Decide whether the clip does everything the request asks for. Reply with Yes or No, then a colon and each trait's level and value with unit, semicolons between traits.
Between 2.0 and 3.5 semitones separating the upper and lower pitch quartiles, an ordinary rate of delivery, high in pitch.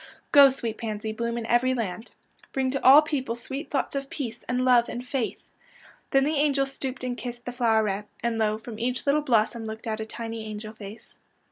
No: average, 3.2 semitones; fast, 210 wpm; high, 240 Hz